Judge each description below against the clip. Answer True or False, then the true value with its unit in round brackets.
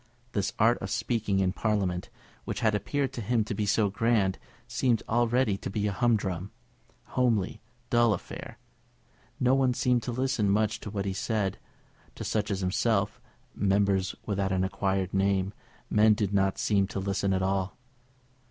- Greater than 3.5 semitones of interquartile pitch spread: False (3.0 semitones)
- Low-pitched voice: True (105 Hz)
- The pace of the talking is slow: False (165 wpm)